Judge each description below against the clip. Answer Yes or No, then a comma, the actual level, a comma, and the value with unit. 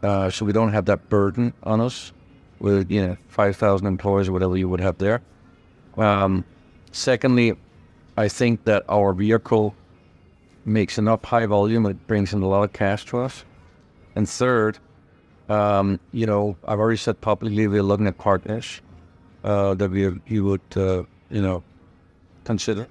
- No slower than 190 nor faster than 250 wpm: No, average, 165 wpm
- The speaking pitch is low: Yes, low, 100 Hz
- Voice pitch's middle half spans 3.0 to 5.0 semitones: No, narrow, 2.5 semitones